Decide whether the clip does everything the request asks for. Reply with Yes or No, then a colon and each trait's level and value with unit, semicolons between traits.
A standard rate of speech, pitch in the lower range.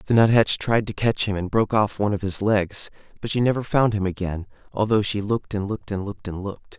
No: fast, 250 wpm; low, 105 Hz